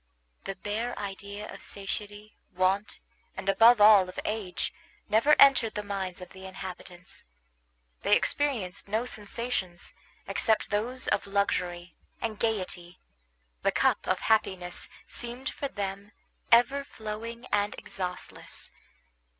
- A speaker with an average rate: No, slow, 120 wpm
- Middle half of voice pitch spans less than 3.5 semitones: Yes, average, 3.1 semitones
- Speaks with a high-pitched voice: Yes, high, 205 Hz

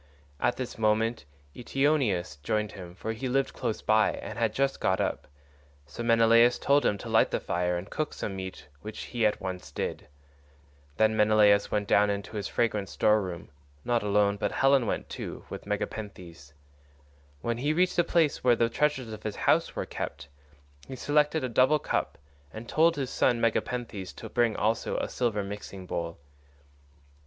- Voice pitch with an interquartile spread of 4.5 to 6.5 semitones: No, average, 3.7 semitones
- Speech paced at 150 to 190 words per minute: Yes, average, 175 wpm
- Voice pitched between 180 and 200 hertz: No, low, 110 Hz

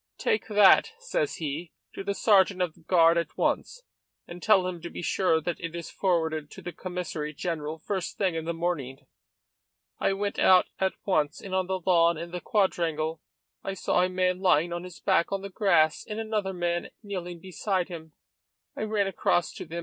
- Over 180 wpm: Yes, average, 195 wpm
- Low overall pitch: No, medium, 180 Hz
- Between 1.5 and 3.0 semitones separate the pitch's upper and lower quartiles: Yes, average, 2.7 semitones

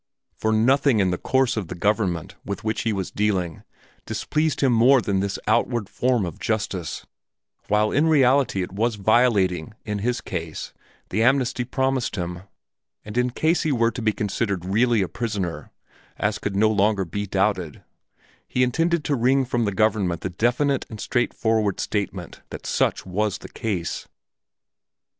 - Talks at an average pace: Yes, average, 165 wpm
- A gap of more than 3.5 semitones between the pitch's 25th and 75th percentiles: Yes, average, 4.2 semitones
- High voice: No, low, 110 Hz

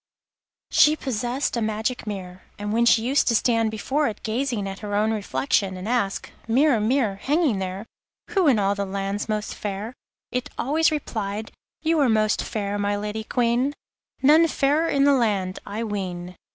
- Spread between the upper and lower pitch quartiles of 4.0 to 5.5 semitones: Yes, average, 4.5 semitones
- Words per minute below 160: No, average, 175 wpm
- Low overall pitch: No, high, 220 Hz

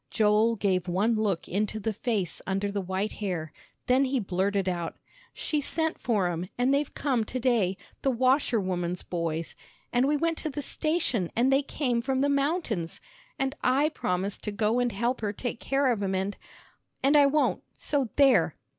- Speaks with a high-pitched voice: Yes, high, 225 Hz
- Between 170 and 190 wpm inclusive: Yes, average, 180 wpm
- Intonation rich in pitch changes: Yes, wide, 5.9 semitones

